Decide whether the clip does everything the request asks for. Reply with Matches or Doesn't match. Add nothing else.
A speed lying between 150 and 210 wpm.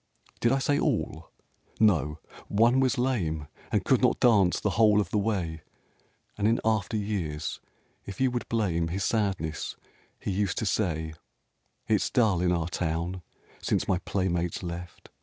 Matches